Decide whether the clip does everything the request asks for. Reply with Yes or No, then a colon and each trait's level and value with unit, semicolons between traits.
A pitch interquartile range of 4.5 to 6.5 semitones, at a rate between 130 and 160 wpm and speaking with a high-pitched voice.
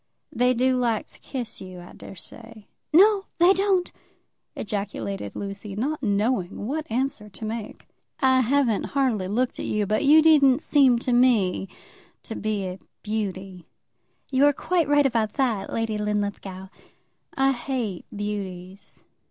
Yes: average, 5.0 semitones; average, 140 wpm; high, 225 Hz